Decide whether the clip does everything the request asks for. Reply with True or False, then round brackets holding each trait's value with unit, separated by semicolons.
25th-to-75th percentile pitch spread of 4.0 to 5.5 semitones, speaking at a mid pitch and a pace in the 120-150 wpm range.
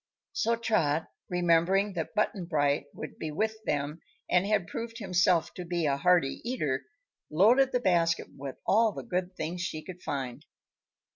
False (5.2 semitones; 175 Hz; 160 wpm)